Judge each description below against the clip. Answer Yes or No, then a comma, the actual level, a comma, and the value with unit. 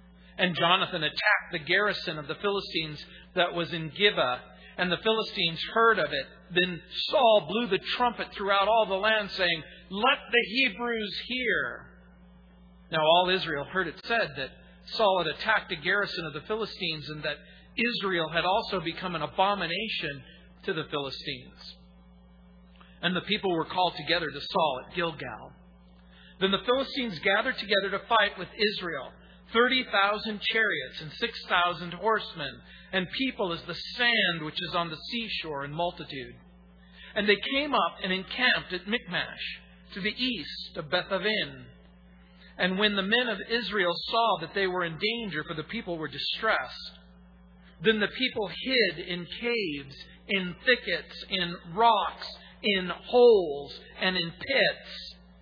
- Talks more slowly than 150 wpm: No, average, 155 wpm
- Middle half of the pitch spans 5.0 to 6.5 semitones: Yes, average, 5.3 semitones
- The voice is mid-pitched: Yes, medium, 180 Hz